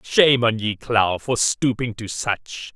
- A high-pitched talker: No, low, 110 Hz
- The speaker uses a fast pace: No, average, 175 wpm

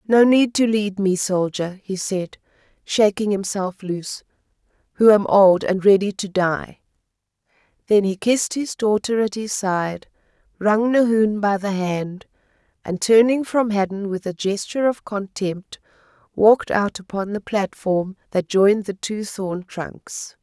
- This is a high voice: Yes, high, 200 Hz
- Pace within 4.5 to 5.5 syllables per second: No, 4.2 syllables/s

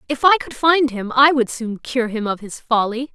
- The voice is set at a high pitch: Yes, very high, 255 Hz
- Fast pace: Yes, fast, 250 wpm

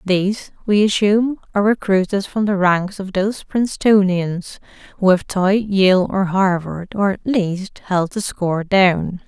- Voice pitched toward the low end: No, high, 195 Hz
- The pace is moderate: Yes, average, 155 wpm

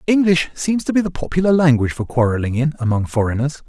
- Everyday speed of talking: Yes, average, 195 wpm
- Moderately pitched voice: Yes, medium, 145 Hz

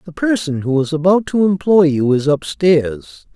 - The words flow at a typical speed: Yes, average, 195 wpm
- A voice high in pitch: No, medium, 165 Hz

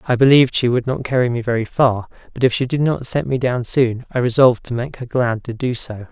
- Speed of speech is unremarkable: No, fast, 265 wpm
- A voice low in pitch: Yes, low, 125 Hz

